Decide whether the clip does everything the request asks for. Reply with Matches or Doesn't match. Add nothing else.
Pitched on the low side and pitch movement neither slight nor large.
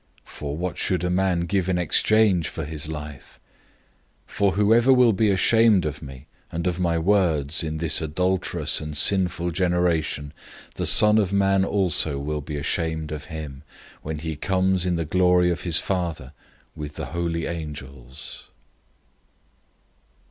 Matches